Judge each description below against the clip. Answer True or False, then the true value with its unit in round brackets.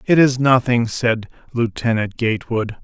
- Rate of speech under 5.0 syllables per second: True (4.6 syllables/s)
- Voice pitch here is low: True (120 Hz)